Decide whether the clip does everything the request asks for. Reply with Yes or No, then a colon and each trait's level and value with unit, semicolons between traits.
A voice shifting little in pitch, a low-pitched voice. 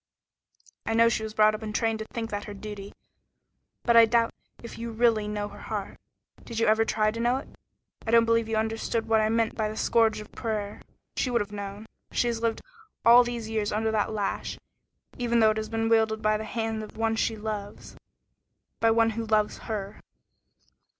No: narrow, 1.2 semitones; high, 220 Hz